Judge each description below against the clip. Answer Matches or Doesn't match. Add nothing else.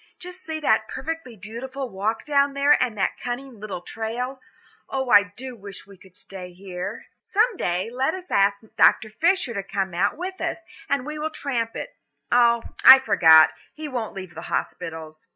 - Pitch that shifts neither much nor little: Doesn't match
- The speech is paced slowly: Doesn't match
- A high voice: Matches